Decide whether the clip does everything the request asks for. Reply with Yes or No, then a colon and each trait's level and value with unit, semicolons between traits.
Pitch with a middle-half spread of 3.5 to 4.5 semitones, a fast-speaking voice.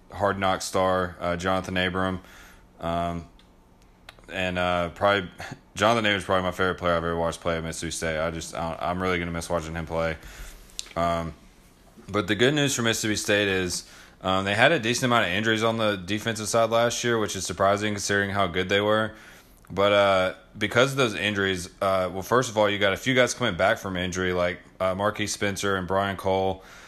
No: average, 2.9 semitones; fast, 210 wpm